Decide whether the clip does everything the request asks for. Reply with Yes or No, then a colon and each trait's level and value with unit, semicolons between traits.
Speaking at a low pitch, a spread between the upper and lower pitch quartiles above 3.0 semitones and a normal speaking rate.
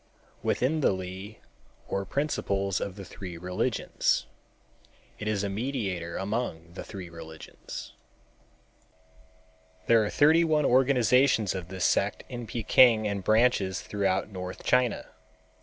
No: low, 100 Hz; average, 4.8 semitones; slow, 125 wpm